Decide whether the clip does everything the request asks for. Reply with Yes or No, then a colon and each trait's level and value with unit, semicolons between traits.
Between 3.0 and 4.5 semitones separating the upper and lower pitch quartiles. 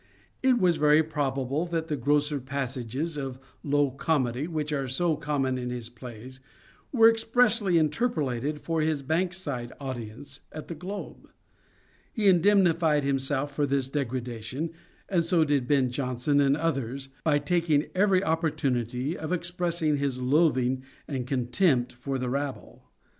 Yes: average, 4.0 semitones